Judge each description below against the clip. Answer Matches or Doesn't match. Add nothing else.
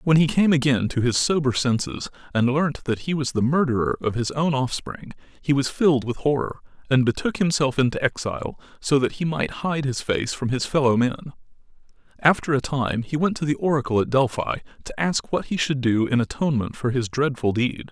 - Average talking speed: Doesn't match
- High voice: Doesn't match